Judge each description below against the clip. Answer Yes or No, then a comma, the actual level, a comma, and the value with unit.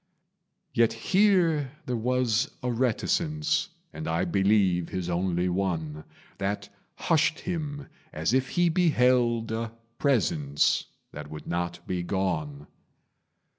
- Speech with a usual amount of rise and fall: No, wide, 8.4 semitones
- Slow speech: Yes, slow, 115 wpm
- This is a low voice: Yes, low, 110 Hz